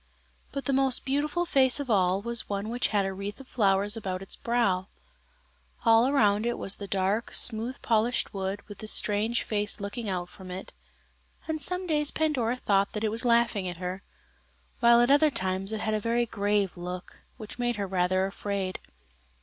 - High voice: Yes, high, 215 Hz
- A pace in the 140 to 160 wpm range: No, average, 185 wpm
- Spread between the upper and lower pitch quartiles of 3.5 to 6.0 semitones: Yes, average, 3.8 semitones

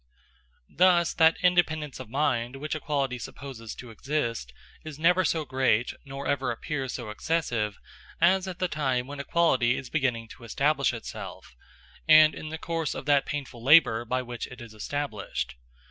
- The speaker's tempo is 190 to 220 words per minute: No, average, 160 wpm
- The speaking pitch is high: No, low, 135 Hz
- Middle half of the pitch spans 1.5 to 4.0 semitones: No, average, 4.5 semitones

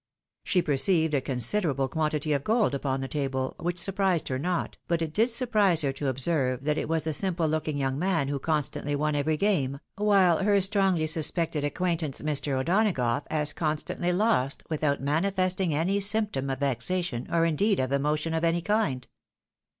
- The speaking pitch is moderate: Yes, medium, 155 Hz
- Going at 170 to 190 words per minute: Yes, average, 175 wpm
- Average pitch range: Yes, average, 4.7 semitones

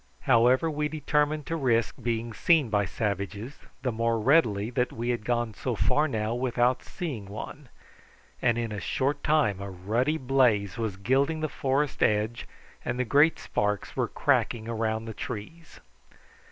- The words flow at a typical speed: Yes, average, 160 wpm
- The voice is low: Yes, low, 120 Hz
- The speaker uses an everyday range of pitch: Yes, average, 4.4 semitones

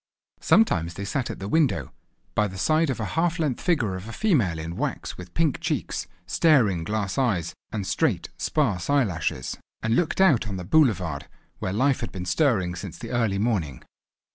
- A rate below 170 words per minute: No, average, 185 wpm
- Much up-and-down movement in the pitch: Yes, wide, 7.8 semitones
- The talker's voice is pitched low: Yes, low, 110 Hz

